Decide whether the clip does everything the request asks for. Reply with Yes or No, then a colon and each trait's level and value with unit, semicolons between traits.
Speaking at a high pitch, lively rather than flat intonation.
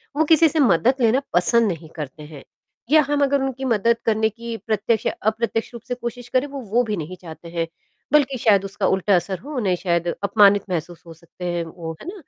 Yes: high, 215 Hz; wide, 6.2 semitones